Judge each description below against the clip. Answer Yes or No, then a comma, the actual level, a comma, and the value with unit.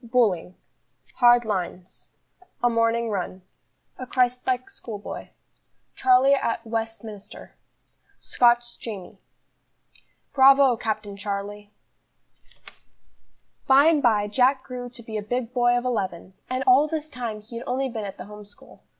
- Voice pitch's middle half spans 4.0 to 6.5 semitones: No, average, 3.4 semitones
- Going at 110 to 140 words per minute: Yes, slow, 135 wpm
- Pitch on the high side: Yes, high, 235 Hz